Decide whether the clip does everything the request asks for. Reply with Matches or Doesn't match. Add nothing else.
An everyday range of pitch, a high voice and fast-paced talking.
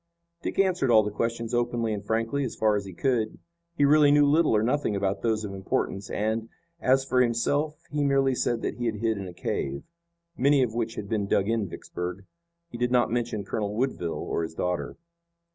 Doesn't match